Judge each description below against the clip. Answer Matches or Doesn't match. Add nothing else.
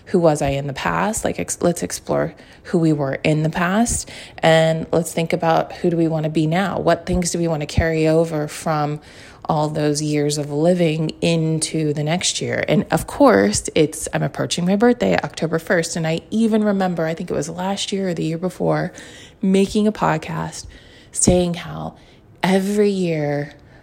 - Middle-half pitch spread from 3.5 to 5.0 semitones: Doesn't match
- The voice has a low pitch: Doesn't match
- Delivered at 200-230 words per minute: Doesn't match